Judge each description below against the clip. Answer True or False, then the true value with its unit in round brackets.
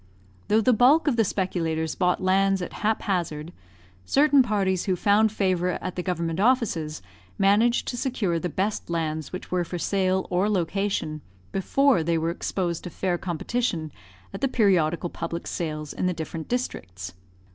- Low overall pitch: False (185 Hz)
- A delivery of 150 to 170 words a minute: True (160 wpm)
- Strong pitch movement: False (3.8 semitones)